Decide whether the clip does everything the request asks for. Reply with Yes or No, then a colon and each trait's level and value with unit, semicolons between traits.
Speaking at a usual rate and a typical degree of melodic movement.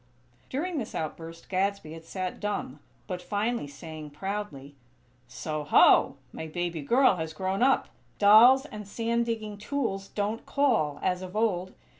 No: average, 145 wpm; wide, 5.7 semitones